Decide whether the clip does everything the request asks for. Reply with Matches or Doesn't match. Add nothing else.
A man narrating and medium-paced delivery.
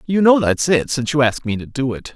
Doesn't match